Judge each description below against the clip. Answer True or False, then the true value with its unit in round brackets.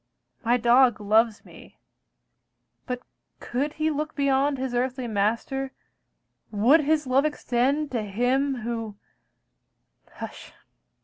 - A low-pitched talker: False (255 Hz)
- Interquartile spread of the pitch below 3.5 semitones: True (3.1 semitones)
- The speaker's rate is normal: False (110 wpm)